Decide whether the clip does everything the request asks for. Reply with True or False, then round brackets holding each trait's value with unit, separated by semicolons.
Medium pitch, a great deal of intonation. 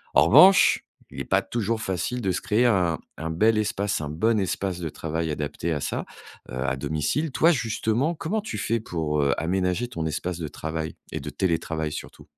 False (90 Hz; 6.2 semitones)